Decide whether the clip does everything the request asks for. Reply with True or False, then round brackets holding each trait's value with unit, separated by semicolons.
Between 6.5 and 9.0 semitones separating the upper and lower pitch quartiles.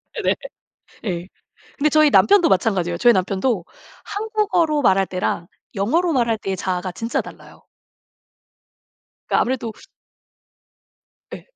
True (8.4 semitones)